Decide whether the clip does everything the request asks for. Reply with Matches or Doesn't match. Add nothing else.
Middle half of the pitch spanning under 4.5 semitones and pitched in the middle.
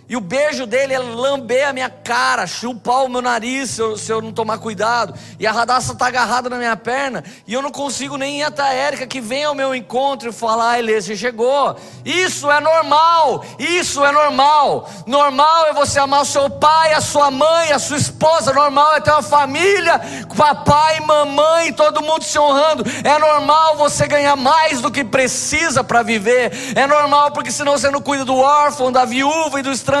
Doesn't match